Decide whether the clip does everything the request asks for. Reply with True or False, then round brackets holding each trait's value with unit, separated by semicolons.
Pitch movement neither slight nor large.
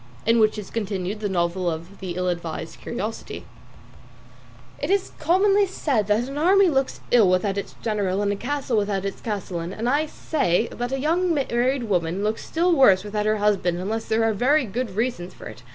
False (5.8 semitones)